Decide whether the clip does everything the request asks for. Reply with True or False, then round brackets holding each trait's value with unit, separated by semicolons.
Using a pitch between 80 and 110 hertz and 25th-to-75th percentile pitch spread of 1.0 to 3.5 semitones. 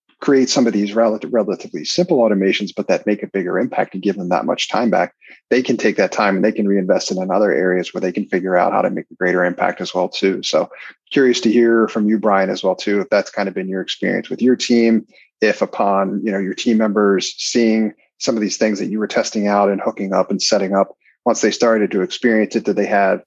True (105 Hz; 2.6 semitones)